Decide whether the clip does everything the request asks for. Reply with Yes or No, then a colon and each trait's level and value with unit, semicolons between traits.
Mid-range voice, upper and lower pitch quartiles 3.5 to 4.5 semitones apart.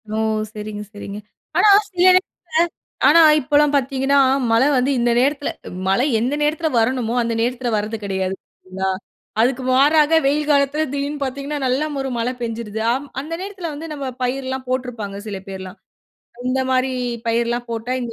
No: very high, 255 Hz; average, 4.0 semitones